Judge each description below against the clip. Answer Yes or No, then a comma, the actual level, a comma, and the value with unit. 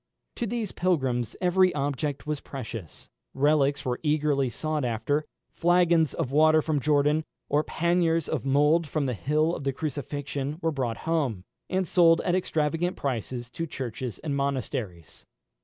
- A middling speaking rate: Yes, average, 150 wpm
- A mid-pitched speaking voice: Yes, medium, 150 Hz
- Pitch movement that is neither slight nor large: Yes, average, 3.4 semitones